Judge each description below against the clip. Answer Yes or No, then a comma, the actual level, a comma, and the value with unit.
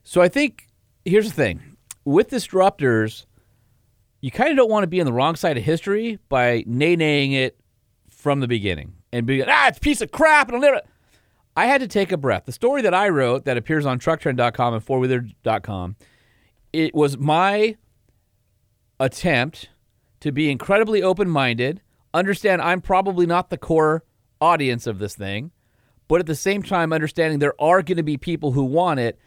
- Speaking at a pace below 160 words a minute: No, average, 180 wpm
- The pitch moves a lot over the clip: Yes, wide, 7.1 semitones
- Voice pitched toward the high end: No, medium, 140 Hz